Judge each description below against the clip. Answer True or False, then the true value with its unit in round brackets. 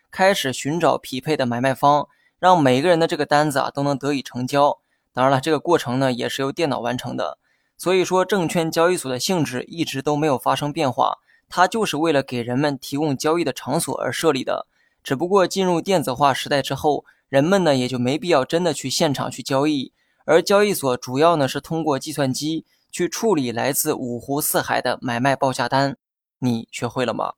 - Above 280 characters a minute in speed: True (310 characters per minute)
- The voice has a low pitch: False (145 Hz)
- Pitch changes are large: False (4.0 semitones)